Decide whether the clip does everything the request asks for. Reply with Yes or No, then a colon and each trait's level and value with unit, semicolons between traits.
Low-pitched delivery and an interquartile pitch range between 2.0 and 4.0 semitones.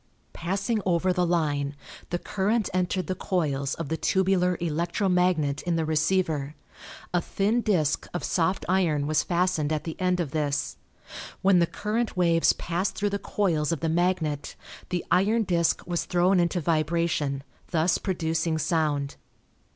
No: medium, 170 Hz; average, 2.9 semitones